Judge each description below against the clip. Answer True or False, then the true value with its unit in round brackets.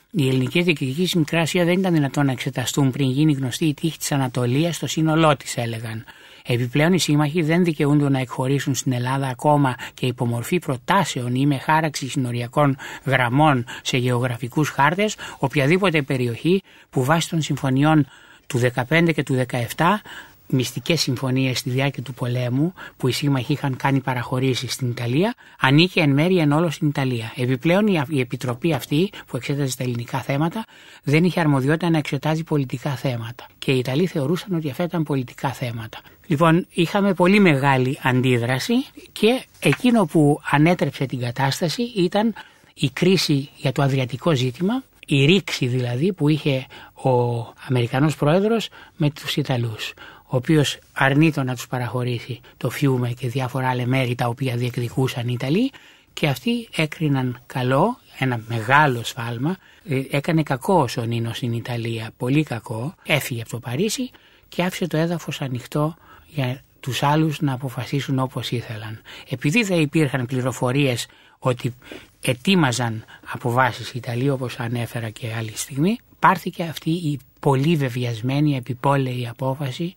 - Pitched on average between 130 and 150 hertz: True (140 Hz)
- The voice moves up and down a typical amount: True (3.9 semitones)